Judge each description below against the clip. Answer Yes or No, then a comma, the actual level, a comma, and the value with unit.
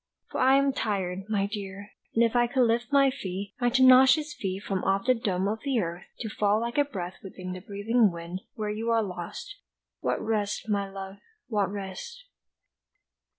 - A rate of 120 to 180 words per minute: No, average, 190 wpm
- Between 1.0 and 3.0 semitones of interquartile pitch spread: No, average, 4.0 semitones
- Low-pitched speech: No, high, 210 Hz